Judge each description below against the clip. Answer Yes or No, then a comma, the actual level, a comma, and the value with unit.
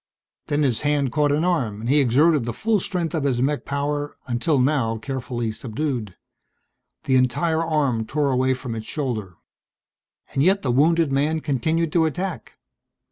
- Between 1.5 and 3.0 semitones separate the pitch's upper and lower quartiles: No, average, 4.1 semitones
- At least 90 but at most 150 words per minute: No, average, 165 wpm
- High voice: No, medium, 140 Hz